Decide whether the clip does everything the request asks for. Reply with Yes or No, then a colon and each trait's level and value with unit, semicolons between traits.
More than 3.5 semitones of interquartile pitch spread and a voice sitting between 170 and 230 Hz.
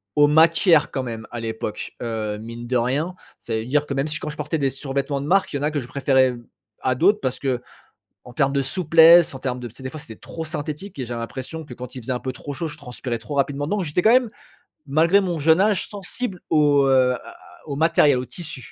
No: average, 4.2 semitones; medium, 140 Hz